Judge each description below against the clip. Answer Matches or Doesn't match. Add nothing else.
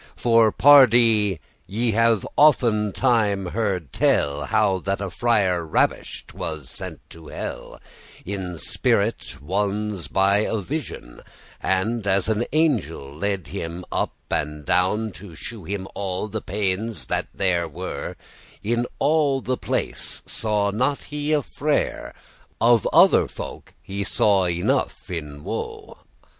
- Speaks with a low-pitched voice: Matches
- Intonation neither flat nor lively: Matches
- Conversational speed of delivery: Doesn't match